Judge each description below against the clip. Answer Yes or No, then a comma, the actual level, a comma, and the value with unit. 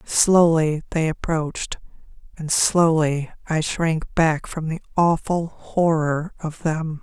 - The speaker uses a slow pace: Yes, slow, 120 wpm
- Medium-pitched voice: Yes, medium, 160 Hz